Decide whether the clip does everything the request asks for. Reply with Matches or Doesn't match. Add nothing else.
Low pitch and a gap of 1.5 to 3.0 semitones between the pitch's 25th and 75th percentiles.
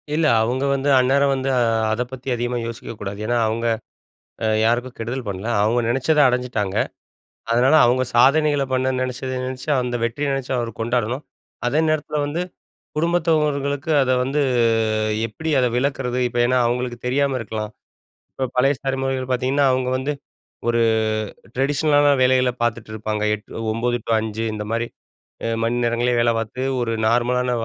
Matches